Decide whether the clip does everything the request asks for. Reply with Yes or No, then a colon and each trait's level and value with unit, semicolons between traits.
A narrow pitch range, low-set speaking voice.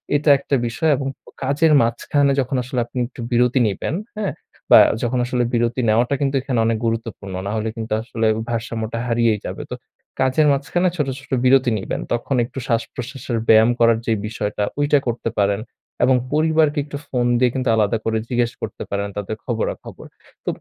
No: average, 3.2 semitones; low, 120 Hz